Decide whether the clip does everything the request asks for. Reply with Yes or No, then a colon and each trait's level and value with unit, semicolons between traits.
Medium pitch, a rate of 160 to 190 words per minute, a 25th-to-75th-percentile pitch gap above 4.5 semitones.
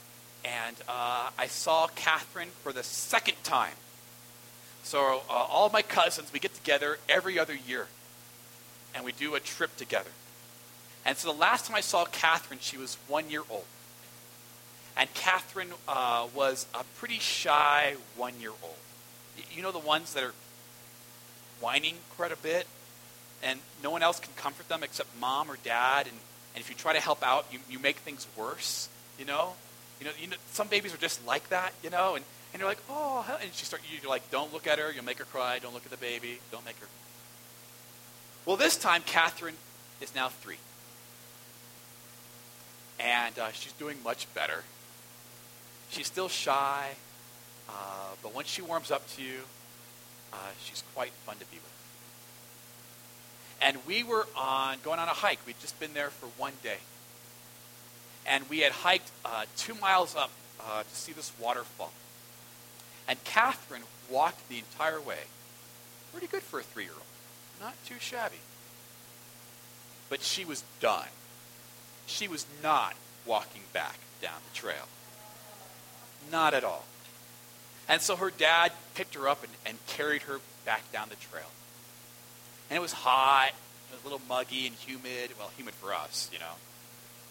No: low, 130 Hz; average, 170 wpm; average, 5.0 semitones